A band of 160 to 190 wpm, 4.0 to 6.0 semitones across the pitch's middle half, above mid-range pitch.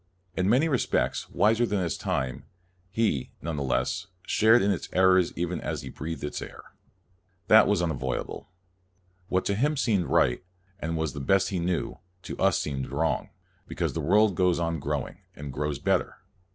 No: average, 170 wpm; average, 5.2 semitones; very low, 85 Hz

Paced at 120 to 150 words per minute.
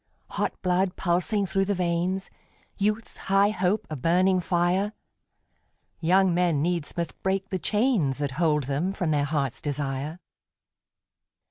Yes: slow, 135 wpm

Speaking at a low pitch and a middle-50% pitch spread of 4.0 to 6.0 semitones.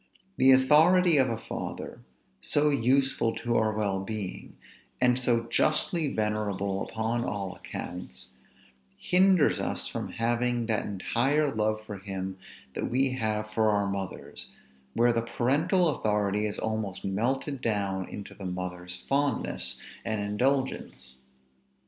Yes: low, 110 Hz; average, 4.7 semitones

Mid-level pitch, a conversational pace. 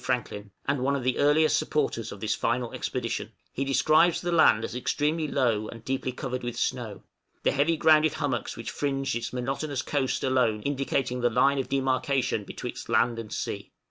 No: low, 130 Hz; average, 180 wpm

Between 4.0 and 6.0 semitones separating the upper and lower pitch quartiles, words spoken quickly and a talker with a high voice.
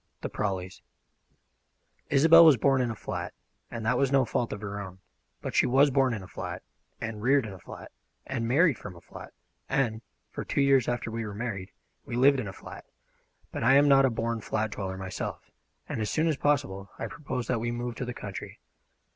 No: average, 4.3 semitones; fast, 215 wpm; low, 120 Hz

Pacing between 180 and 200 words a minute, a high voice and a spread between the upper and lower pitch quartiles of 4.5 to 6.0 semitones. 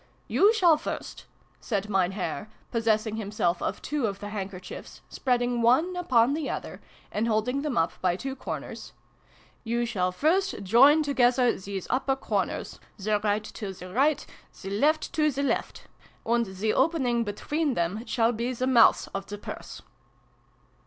No: average, 165 wpm; high, 235 Hz; average, 5.0 semitones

